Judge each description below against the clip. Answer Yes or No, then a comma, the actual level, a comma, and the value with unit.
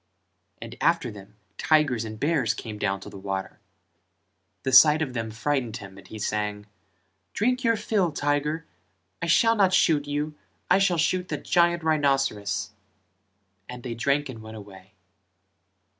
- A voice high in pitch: No, medium, 140 Hz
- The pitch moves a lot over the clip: Yes, wide, 7.0 semitones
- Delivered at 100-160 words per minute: Yes, average, 155 wpm